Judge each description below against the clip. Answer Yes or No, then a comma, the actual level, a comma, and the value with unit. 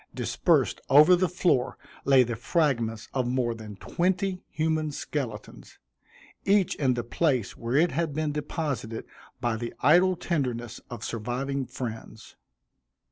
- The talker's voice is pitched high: No, low, 135 Hz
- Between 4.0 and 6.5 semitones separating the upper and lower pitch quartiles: Yes, average, 5.2 semitones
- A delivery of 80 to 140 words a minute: Yes, slow, 135 wpm